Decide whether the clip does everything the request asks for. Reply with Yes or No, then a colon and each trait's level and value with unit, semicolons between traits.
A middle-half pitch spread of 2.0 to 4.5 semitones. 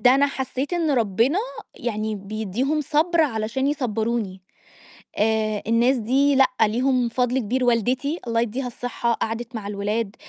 Yes: average, 3.5 semitones